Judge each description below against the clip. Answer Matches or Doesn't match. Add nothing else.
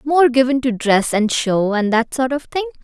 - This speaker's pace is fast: Matches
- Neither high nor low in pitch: Doesn't match